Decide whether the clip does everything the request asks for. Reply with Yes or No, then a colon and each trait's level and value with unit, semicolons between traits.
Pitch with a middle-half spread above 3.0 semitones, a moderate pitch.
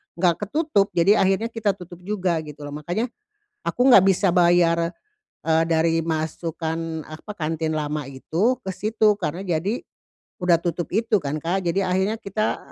Yes: average, 3.6 semitones; medium, 175 Hz